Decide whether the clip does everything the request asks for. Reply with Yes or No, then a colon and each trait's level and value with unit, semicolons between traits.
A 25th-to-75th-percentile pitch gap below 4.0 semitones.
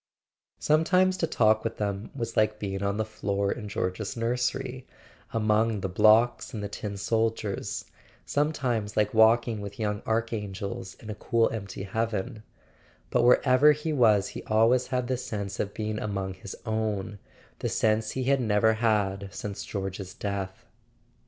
Yes: average, 2.8 semitones